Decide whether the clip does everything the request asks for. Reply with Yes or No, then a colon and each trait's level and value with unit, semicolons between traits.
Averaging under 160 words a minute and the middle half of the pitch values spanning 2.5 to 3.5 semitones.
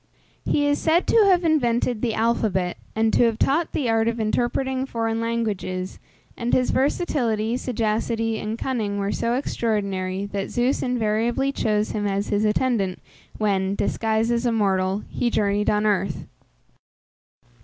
Yes: average, 150 wpm; average, 2.9 semitones